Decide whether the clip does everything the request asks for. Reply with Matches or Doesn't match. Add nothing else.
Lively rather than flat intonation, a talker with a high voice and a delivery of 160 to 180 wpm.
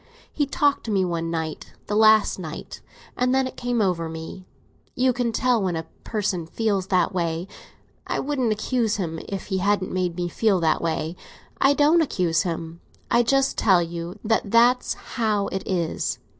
Matches